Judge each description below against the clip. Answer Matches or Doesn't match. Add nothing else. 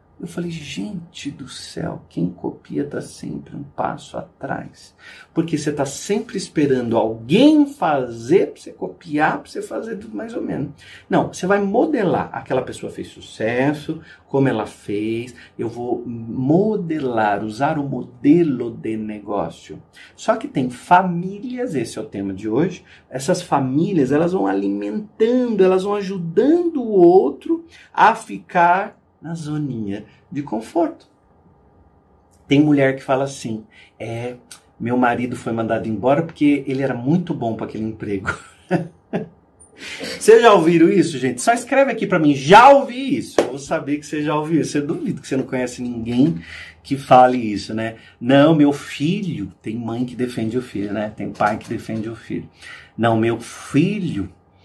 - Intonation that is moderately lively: Doesn't match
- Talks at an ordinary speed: Matches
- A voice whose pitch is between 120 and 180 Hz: Matches